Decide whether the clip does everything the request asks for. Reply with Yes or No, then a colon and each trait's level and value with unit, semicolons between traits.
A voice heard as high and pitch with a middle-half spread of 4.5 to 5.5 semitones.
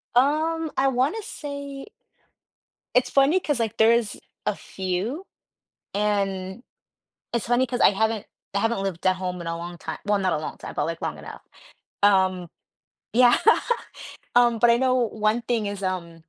Yes: high, 220 Hz; average, 5.1 semitones